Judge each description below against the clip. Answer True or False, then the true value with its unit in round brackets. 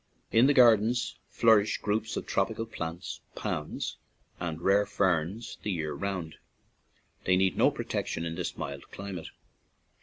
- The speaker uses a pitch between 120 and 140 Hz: False (95 Hz)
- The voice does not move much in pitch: False (4.8 semitones)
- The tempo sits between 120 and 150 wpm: True (140 wpm)